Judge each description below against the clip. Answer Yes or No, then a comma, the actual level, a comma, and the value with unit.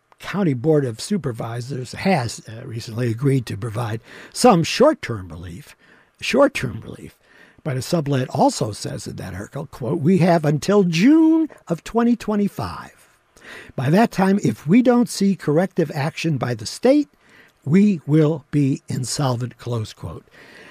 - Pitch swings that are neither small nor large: No, wide, 7.8 semitones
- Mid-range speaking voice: Yes, medium, 155 Hz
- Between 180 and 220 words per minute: No, average, 140 wpm